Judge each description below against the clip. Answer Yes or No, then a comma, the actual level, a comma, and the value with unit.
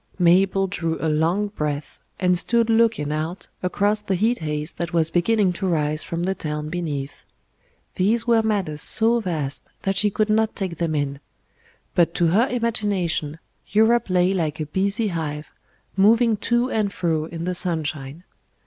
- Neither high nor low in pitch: Yes, medium, 180 Hz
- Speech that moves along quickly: No, average, 165 wpm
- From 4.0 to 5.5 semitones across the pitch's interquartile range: Yes, average, 4.9 semitones